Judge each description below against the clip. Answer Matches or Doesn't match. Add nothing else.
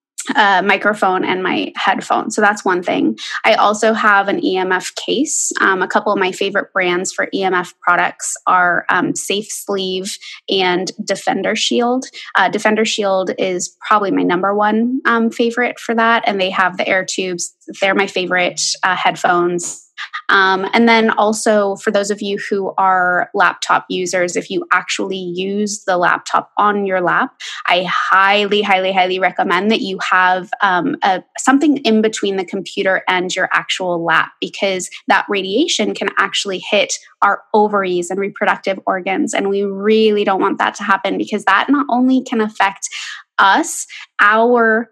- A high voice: Matches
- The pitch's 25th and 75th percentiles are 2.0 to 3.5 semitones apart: Matches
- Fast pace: Doesn't match